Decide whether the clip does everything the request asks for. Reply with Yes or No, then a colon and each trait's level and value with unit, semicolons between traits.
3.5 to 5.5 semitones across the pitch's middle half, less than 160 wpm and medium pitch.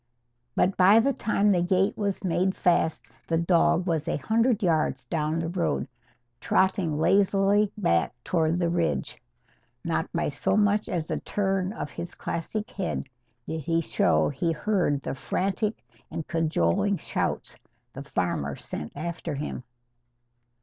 Yes: average, 3.9 semitones; average, 145 wpm; medium, 175 Hz